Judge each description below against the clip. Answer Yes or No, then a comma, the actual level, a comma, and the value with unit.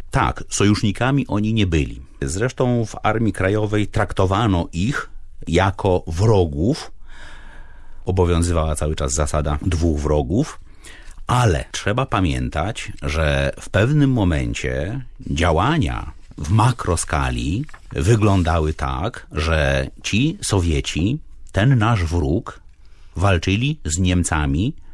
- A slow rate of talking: Yes, slow, 95 wpm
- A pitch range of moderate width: No, wide, 6.0 semitones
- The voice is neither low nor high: No, very low, 90 Hz